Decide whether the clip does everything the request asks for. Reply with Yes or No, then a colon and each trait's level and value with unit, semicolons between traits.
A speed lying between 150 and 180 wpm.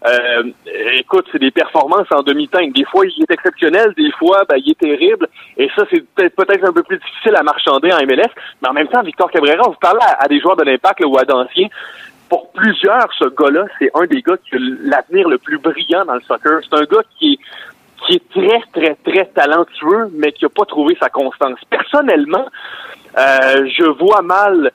No: fast, 220 wpm